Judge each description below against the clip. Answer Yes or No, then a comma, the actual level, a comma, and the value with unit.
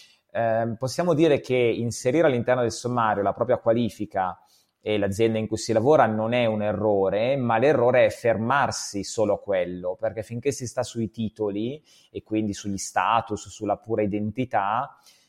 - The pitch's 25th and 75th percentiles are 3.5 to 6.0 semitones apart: No, narrow, 2.5 semitones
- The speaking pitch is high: No, low, 110 Hz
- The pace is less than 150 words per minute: No, average, 160 wpm